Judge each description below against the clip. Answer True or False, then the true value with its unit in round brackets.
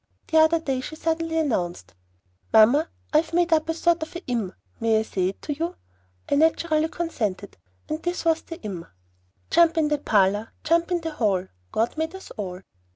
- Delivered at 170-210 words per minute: True (195 wpm)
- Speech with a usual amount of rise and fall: False (7.1 semitones)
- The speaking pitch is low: False (310 Hz)